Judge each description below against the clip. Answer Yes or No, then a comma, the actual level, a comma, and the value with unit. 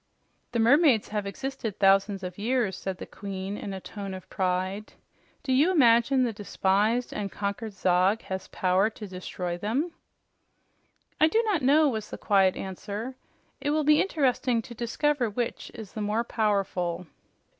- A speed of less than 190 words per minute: Yes, average, 160 wpm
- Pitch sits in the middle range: No, high, 215 Hz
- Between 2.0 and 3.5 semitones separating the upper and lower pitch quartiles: No, average, 4.8 semitones